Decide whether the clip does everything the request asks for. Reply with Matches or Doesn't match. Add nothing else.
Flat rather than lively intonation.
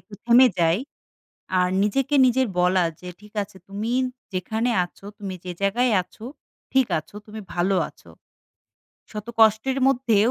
Doesn't match